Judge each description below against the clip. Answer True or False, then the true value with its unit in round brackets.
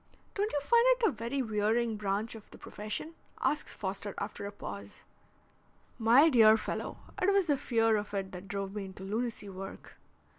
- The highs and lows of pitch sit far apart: False (4.0 semitones)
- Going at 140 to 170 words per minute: False (180 wpm)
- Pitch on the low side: False (220 Hz)